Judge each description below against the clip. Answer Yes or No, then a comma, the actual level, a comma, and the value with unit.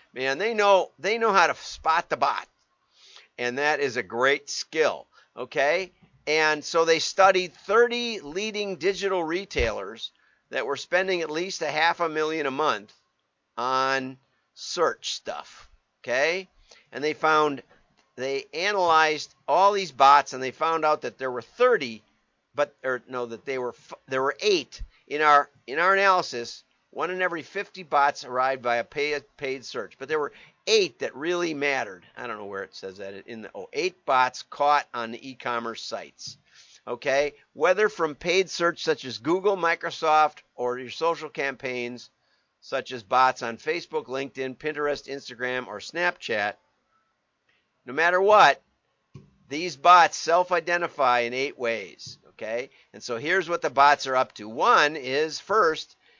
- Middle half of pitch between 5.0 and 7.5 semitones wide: Yes, average, 5.3 semitones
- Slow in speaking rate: No, average, 160 wpm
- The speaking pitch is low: No, medium, 150 Hz